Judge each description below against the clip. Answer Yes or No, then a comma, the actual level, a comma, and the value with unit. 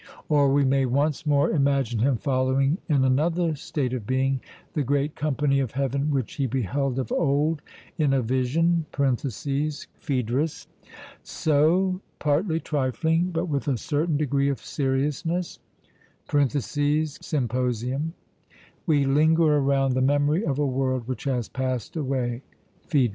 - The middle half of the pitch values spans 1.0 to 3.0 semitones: Yes, narrow, 2.5 semitones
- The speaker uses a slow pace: Yes, slow, 130 wpm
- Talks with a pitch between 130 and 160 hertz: Yes, medium, 140 Hz